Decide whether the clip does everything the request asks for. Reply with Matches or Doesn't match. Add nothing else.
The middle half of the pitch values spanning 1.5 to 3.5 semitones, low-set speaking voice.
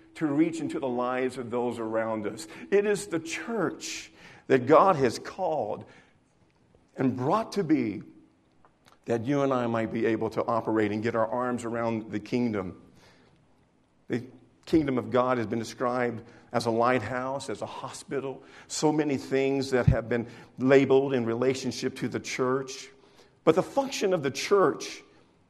Matches